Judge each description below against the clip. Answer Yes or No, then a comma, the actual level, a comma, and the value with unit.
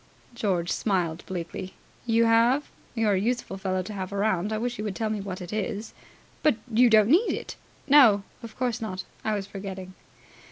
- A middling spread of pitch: Yes, average, 3.3 semitones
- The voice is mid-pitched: No, high, 210 Hz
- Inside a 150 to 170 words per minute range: No, average, 190 wpm